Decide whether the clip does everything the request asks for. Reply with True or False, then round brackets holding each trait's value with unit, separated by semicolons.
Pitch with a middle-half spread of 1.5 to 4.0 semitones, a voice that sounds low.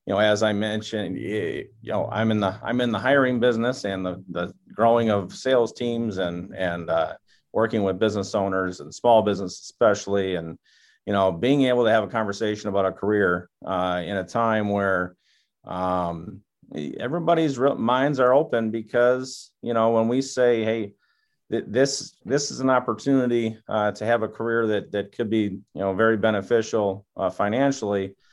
True (3.5 semitones; 110 Hz)